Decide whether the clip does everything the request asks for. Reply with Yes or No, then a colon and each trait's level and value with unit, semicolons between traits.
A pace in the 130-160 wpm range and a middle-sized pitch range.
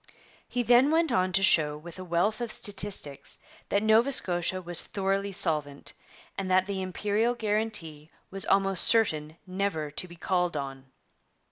Yes: average, 155 wpm; average, 4.0 semitones